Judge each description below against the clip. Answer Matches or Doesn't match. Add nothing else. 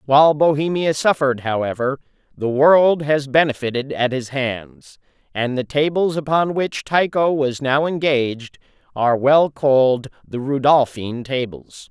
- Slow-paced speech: Matches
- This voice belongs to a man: Matches